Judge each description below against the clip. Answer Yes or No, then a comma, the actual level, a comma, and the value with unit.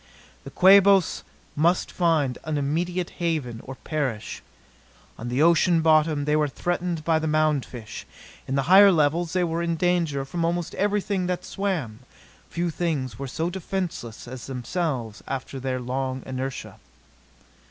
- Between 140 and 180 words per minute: Yes, average, 150 wpm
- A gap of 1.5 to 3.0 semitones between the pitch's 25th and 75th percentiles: No, average, 4.7 semitones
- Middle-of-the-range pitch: Yes, medium, 155 Hz